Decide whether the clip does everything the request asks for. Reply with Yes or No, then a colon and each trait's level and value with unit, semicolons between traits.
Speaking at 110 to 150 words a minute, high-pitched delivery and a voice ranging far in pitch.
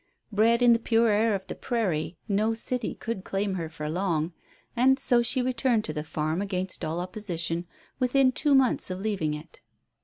No: average, 185 wpm; high, 205 Hz; wide, 5.7 semitones